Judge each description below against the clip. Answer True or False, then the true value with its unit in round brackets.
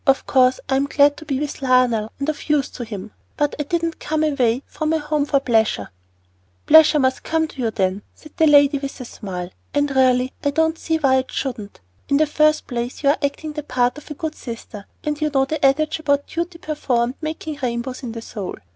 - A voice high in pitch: True (280 Hz)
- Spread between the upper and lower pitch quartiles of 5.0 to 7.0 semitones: False (3.5 semitones)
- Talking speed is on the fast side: True (220 wpm)